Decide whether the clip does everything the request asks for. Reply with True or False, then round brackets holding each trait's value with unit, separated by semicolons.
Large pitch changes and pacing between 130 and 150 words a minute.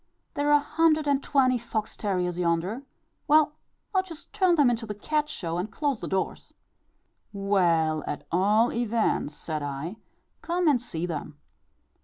False (8.7 semitones; 160 wpm)